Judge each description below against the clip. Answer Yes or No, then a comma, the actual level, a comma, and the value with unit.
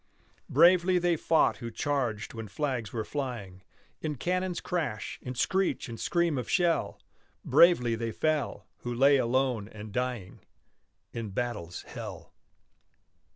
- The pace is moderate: No, slow, 130 wpm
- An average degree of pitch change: No, wide, 6.1 semitones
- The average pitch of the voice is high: No, low, 125 Hz